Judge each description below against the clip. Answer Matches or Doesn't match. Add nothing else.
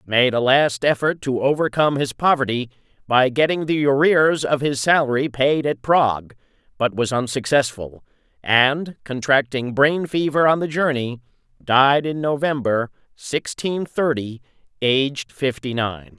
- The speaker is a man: Matches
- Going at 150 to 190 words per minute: Doesn't match